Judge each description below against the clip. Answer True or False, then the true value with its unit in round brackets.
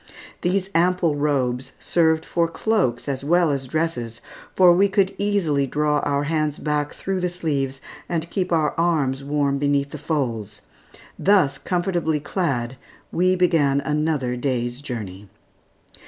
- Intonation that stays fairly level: False (4.2 semitones)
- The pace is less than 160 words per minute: True (140 wpm)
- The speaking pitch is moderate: True (150 Hz)